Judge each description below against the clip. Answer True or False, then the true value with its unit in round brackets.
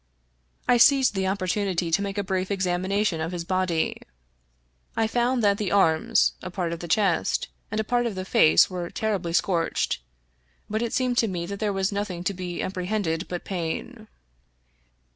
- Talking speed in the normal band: True (180 wpm)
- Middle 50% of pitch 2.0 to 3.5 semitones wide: True (3.2 semitones)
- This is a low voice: False (190 Hz)